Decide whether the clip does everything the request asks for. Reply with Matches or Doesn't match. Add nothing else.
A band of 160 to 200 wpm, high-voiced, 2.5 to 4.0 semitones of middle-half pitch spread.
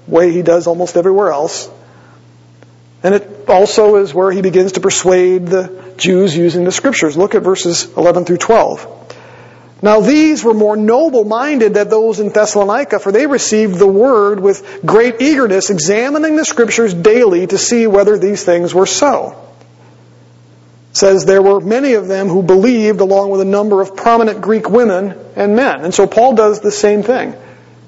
Matches